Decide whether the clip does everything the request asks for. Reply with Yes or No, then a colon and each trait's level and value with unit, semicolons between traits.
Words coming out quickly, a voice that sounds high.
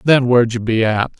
No: fast, 250 wpm; low, 120 Hz